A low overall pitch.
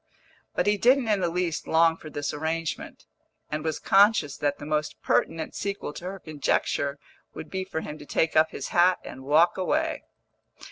No: medium, 165 Hz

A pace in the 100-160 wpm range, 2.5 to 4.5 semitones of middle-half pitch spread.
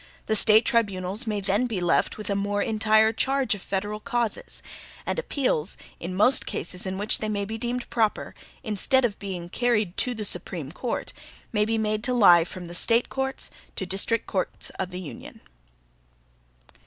No: average, 180 wpm; average, 3.4 semitones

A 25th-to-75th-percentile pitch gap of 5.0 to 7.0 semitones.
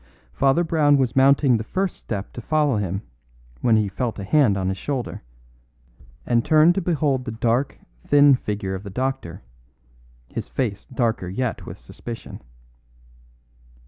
Yes: average, 5.3 semitones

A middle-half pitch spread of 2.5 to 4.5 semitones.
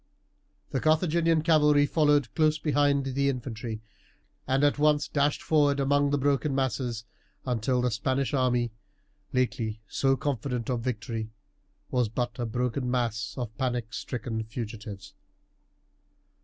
Yes: average, 3.5 semitones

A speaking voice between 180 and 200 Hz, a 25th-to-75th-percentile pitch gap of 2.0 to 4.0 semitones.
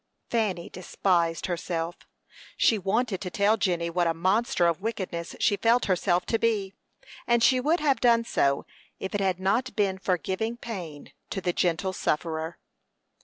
No: high, 190 Hz; average, 4.7 semitones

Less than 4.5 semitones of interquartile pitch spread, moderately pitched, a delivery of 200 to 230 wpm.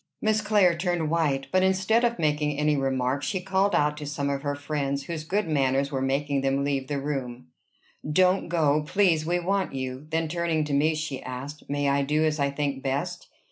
Yes: average, 3.5 semitones; medium, 150 Hz; fast, 205 wpm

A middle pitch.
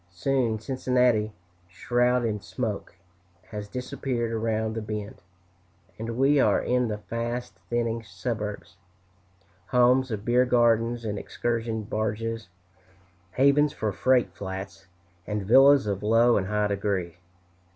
No: low, 115 Hz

